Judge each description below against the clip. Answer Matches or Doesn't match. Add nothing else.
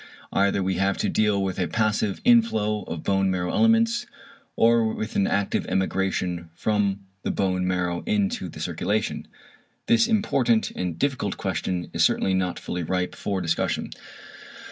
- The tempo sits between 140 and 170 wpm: Matches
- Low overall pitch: Matches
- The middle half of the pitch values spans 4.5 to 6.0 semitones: Doesn't match